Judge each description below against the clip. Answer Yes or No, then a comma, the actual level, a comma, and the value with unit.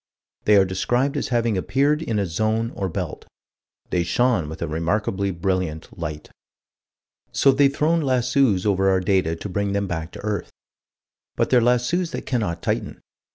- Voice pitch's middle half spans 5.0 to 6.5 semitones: Yes, wide, 5.4 semitones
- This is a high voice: No, low, 100 Hz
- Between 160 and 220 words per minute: Yes, average, 165 wpm